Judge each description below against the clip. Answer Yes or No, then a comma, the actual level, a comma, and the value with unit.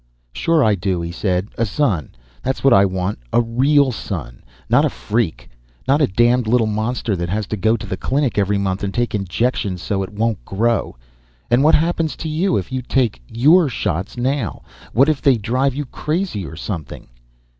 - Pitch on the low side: Yes, low, 115 Hz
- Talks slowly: No, average, 195 wpm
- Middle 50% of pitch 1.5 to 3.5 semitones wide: No, wide, 5.5 semitones